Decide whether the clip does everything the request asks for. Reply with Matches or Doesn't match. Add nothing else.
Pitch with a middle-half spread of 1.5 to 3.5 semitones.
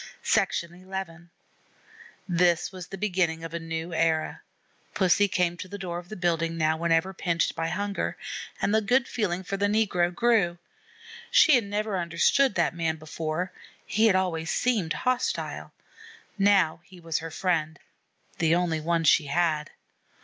Matches